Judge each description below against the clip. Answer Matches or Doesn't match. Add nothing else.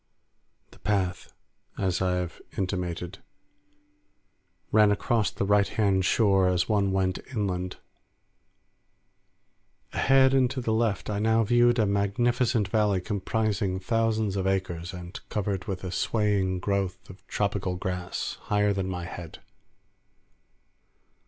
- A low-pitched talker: Matches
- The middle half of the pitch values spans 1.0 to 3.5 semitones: Matches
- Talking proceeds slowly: Matches